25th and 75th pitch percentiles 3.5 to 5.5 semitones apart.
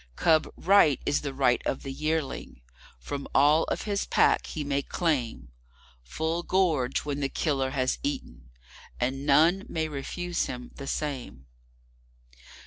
Yes: average, 4.0 semitones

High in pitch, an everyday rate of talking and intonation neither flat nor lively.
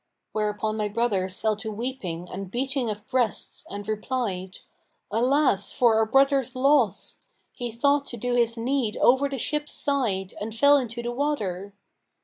Yes: high, 235 Hz; average, 155 wpm; average, 4.2 semitones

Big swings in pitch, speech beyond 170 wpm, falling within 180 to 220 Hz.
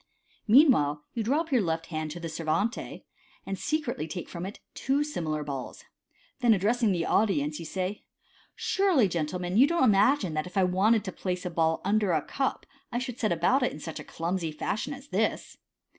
Yes: wide, 7.0 semitones; fast, 205 wpm; high, 190 Hz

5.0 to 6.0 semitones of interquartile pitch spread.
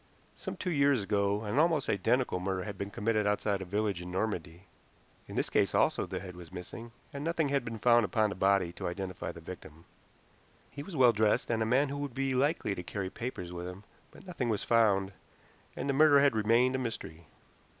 Yes: wide, 5.4 semitones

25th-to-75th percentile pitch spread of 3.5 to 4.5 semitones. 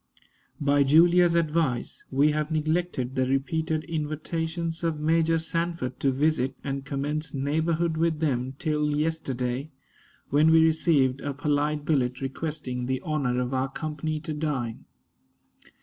No: average, 3.0 semitones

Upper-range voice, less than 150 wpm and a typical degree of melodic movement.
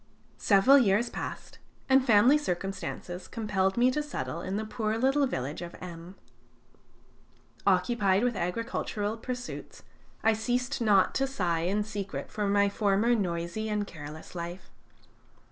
Yes: high, 205 Hz; slow, 135 wpm; average, 4.4 semitones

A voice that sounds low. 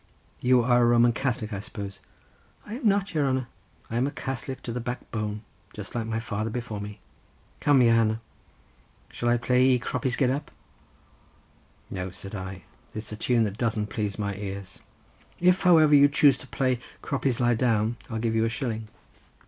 Yes: low, 120 Hz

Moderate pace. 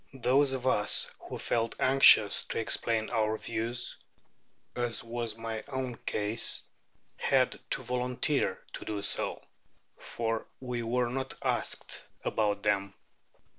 No: slow, 125 wpm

